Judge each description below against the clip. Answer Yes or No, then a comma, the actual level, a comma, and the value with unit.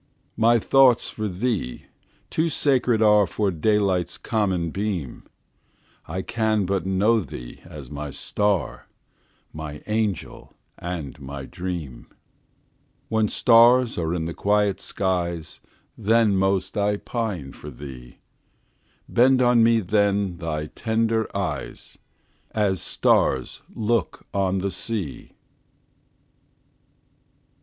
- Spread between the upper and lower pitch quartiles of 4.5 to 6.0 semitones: Yes, average, 4.8 semitones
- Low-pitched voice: Yes, low, 100 Hz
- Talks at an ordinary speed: No, slow, 95 wpm